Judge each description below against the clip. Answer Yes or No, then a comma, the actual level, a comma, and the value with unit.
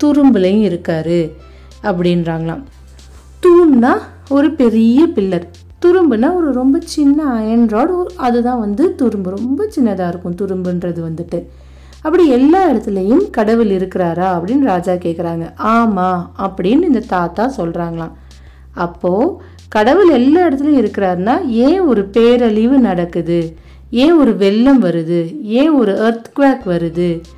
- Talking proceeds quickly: No, average, 105 wpm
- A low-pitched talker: No, high, 215 Hz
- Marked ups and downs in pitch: Yes, wide, 7.6 semitones